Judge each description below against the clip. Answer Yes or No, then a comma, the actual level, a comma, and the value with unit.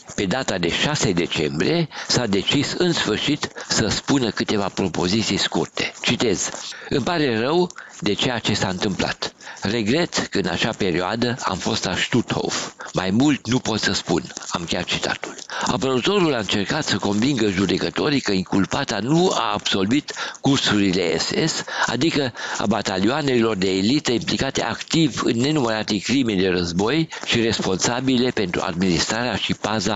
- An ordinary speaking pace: Yes, average, 145 wpm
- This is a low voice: Yes, low, 110 Hz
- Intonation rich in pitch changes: Yes, wide, 5.8 semitones